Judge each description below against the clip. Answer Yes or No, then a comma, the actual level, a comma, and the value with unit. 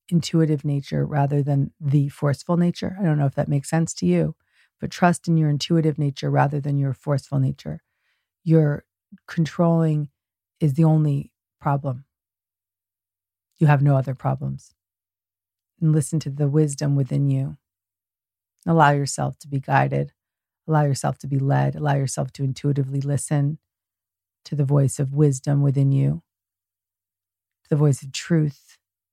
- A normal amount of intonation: No, wide, 7.7 semitones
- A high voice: No, medium, 140 Hz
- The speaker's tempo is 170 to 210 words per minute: No, average, 145 wpm